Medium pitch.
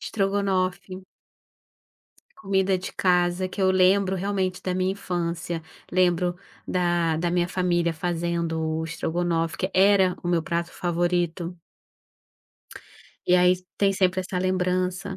Yes: medium, 180 Hz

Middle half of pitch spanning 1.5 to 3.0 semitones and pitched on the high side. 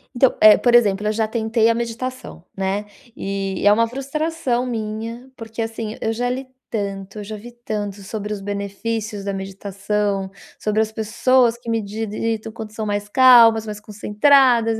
Yes: narrow, 2.4 semitones; high, 220 Hz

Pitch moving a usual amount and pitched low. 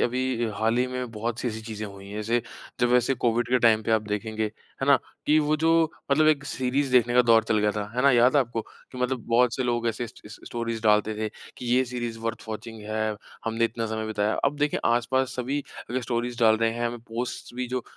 No: narrow, 2.3 semitones; low, 120 Hz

